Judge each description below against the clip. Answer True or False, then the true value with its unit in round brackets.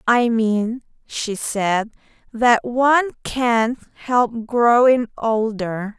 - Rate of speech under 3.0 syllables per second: True (2.7 syllables/s)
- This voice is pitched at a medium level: False (230 Hz)